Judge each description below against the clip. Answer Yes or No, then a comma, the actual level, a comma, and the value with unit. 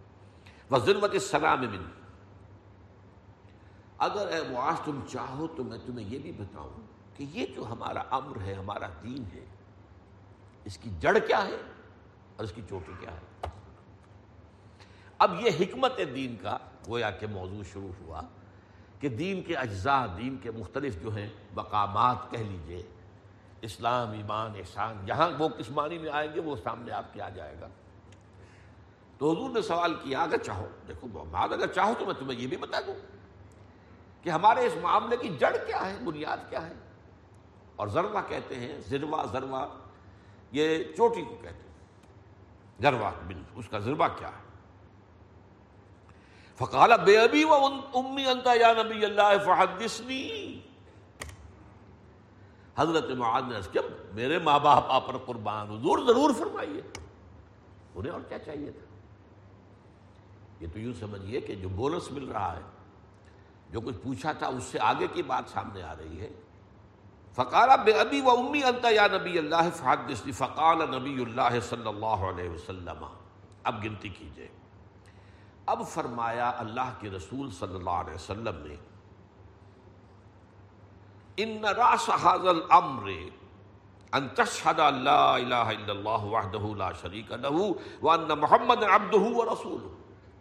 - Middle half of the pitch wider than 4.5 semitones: Yes, average, 5.1 semitones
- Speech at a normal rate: Yes, average, 140 wpm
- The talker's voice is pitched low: Yes, low, 105 Hz